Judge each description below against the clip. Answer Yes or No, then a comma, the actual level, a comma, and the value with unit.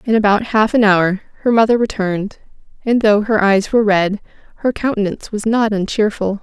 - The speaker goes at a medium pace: Yes, average, 175 wpm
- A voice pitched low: No, high, 210 Hz